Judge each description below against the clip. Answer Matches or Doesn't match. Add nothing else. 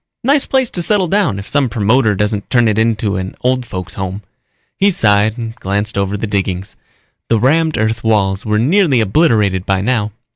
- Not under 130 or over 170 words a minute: Doesn't match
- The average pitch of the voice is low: Matches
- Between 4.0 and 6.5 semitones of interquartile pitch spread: Matches